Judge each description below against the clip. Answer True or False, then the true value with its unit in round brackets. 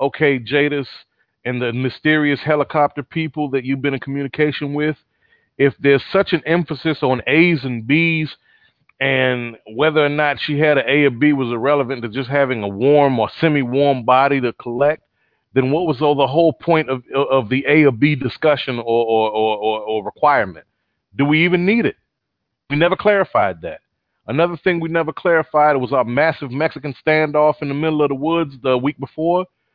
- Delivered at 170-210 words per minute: True (185 wpm)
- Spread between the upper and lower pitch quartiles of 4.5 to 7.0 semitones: False (2.8 semitones)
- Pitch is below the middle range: False (145 Hz)